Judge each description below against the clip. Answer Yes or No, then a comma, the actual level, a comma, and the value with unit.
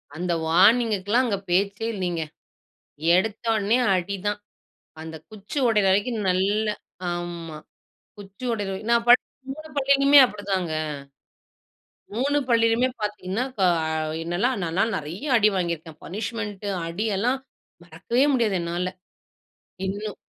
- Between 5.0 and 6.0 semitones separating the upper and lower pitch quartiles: No, average, 4.1 semitones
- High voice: Yes, high, 205 Hz